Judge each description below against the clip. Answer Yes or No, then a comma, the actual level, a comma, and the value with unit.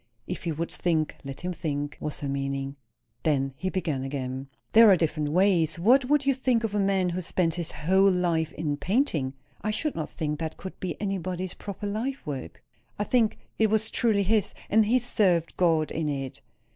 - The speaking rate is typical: Yes, average, 195 wpm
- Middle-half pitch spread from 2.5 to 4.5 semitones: No, wide, 5.5 semitones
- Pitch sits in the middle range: Yes, medium, 175 Hz